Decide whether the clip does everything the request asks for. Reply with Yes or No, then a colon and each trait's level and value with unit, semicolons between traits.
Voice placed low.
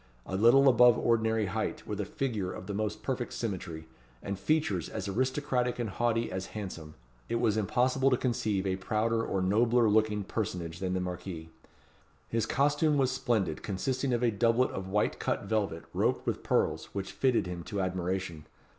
Yes: low, 110 Hz